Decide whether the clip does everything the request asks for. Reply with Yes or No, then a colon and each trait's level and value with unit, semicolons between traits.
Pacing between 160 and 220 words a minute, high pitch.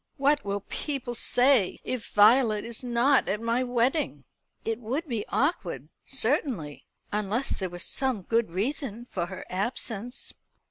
No: average, 140 wpm; high, 235 Hz